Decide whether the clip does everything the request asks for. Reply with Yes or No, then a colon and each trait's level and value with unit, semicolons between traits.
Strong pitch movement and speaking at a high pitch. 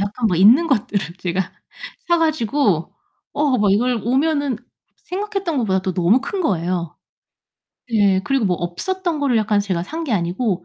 Yes: wide, 7.5 semitones; high, 220 Hz